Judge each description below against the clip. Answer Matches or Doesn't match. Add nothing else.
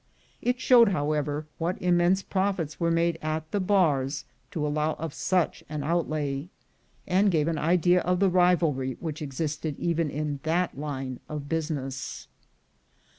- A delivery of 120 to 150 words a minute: Matches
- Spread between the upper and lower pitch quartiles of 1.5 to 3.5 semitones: Matches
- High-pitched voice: Doesn't match